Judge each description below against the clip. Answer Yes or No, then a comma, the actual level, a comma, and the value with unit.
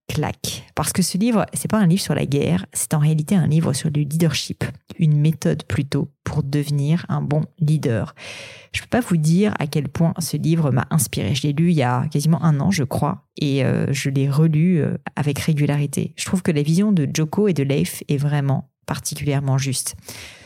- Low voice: No, medium, 150 Hz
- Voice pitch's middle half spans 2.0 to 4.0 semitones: Yes, average, 2.9 semitones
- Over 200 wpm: Yes, average, 210 wpm